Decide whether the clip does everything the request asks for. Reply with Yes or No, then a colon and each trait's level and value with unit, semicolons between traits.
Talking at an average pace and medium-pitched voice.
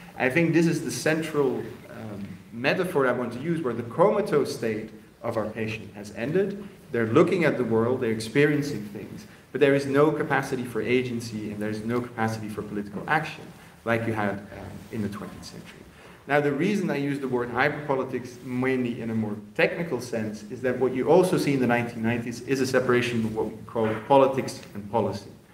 No: average, 195 wpm; low, 120 Hz